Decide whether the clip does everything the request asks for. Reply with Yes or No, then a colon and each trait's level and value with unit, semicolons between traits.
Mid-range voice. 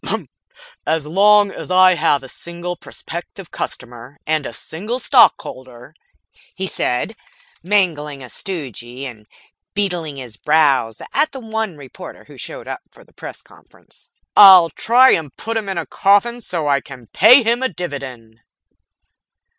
Yes: medium, 165 Hz